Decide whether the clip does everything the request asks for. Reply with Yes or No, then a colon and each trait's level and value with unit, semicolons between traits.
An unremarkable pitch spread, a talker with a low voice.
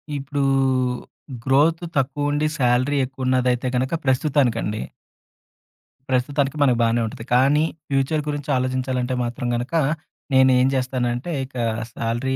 No: narrow, 2.3 semitones; low, 130 Hz